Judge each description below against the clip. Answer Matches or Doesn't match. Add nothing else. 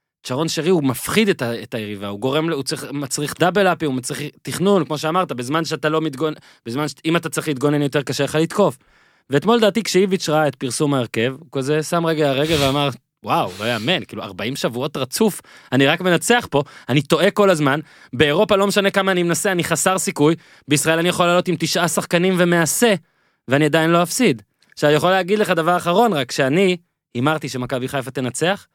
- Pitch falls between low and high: Matches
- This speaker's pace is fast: Matches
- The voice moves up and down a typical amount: Matches